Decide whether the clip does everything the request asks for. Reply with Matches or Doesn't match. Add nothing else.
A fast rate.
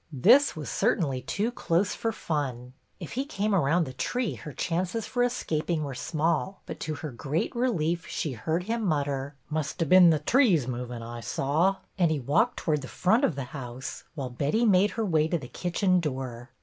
Matches